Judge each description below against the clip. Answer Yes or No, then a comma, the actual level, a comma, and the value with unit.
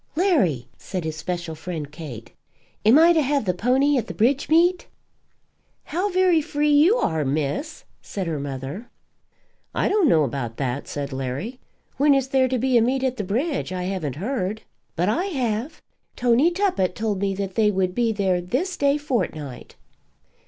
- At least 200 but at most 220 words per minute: No, average, 175 wpm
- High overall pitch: Yes, high, 220 Hz